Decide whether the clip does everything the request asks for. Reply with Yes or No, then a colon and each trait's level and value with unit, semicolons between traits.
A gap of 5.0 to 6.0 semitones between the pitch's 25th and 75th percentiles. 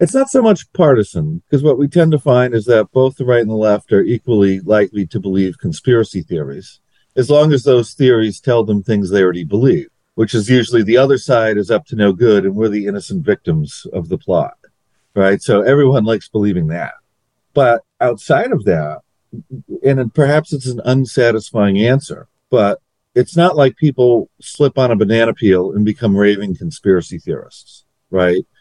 Yes: wide, 5.5 semitones